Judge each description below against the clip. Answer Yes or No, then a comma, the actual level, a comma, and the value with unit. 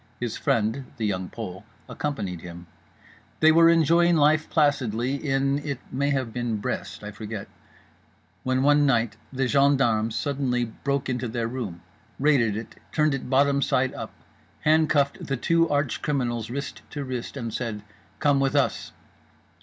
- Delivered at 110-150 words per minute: Yes, average, 145 wpm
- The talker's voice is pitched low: Yes, low, 130 Hz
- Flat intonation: No, average, 4.0 semitones